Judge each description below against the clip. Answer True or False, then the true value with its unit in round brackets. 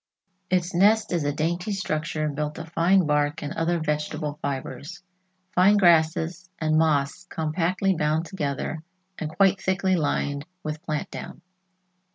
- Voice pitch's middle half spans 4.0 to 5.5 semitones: False (3.1 semitones)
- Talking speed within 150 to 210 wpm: False (140 wpm)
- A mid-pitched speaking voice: True (160 Hz)